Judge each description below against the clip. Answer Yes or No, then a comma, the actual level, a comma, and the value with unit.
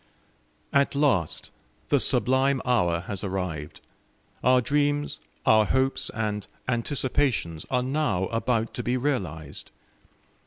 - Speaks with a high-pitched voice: No, low, 120 Hz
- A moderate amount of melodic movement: No, wide, 5.9 semitones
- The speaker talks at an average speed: No, slow, 110 wpm